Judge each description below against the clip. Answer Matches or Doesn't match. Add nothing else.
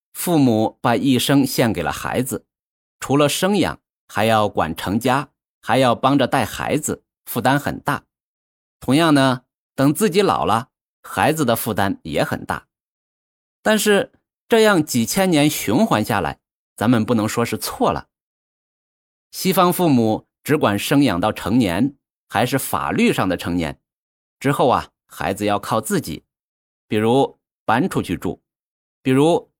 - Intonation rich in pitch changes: Matches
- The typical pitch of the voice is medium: Doesn't match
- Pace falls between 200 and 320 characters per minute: Matches